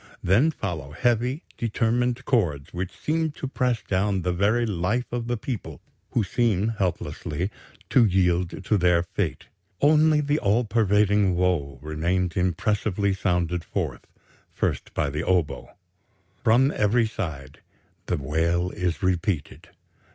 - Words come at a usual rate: No, slow, 130 wpm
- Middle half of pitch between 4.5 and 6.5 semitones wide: Yes, average, 5.1 semitones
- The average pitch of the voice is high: No, very low, 95 Hz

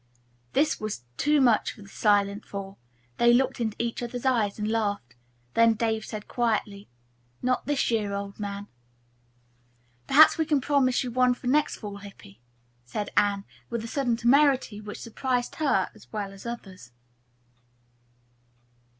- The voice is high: Yes, high, 225 Hz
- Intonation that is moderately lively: Yes, average, 3.8 semitones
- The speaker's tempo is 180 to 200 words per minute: No, average, 155 wpm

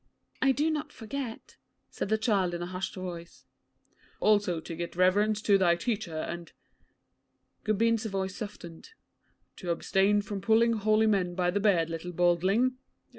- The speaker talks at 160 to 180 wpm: No, average, 150 wpm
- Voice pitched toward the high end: Yes, high, 195 Hz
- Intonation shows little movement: No, average, 3.8 semitones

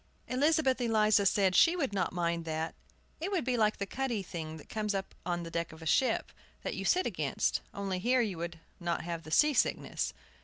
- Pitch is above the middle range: Yes, high, 200 Hz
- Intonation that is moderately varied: No, wide, 6.9 semitones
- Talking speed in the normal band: No, fast, 215 wpm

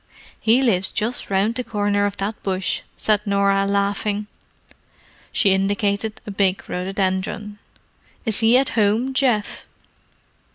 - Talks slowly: Yes, slow, 125 wpm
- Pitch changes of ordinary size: No, narrow, 1.9 semitones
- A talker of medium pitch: No, high, 205 Hz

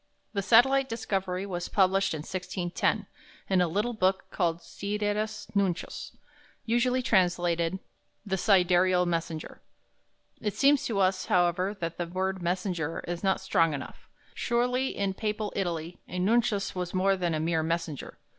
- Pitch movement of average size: Yes, average, 3.0 semitones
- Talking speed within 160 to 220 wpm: No, average, 145 wpm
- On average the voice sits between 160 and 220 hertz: Yes, medium, 185 Hz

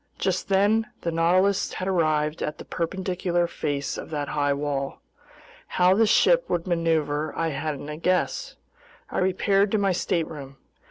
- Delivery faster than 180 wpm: No, average, 155 wpm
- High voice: No, medium, 170 Hz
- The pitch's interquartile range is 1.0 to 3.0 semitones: No, average, 3.9 semitones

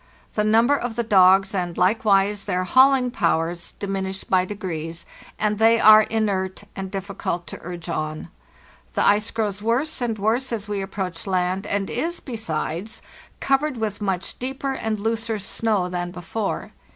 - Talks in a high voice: Yes, high, 205 Hz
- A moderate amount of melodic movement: Yes, average, 3.4 semitones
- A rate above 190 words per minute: No, average, 155 wpm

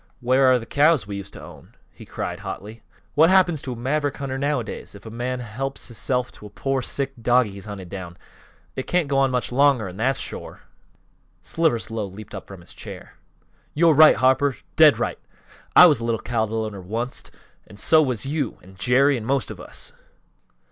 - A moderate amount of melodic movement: Yes, average, 4.3 semitones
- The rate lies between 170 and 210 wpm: Yes, average, 200 wpm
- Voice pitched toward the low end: Yes, low, 125 Hz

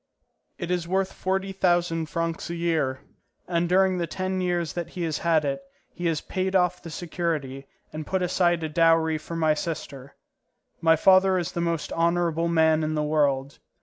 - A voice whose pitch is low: No, medium, 170 Hz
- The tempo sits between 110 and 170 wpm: No, average, 180 wpm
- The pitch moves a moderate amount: No, narrow, 2.2 semitones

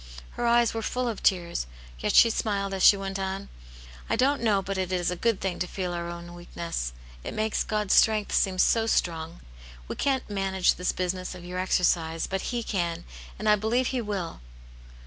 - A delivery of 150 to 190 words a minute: No, fast, 205 wpm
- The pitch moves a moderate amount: Yes, average, 3.6 semitones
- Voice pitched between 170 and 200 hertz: Yes, high, 190 Hz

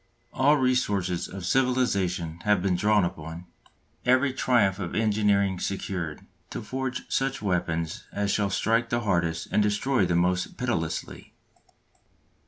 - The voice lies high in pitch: No, low, 100 Hz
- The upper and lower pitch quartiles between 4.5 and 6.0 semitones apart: Yes, average, 5.2 semitones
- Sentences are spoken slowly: Yes, slow, 130 wpm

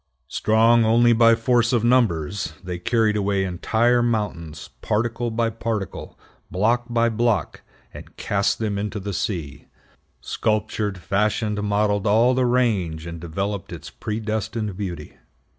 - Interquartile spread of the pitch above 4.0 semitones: No, average, 3.0 semitones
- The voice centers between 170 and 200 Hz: No, low, 105 Hz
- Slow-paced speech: Yes, slow, 130 wpm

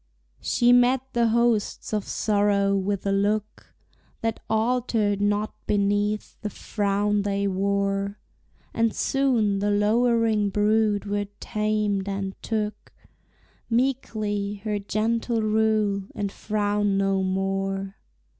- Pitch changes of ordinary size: No, narrow, 1.7 semitones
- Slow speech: Yes, slow, 110 wpm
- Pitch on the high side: Yes, high, 205 Hz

